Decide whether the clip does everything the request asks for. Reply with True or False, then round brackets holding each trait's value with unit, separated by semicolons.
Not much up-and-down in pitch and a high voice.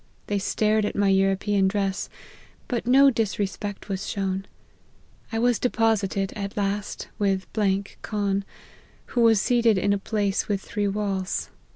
True (1.9 semitones; 205 Hz)